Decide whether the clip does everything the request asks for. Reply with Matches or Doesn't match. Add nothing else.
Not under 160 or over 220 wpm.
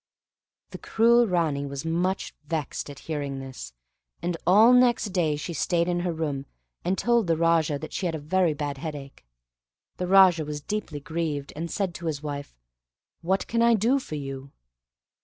Matches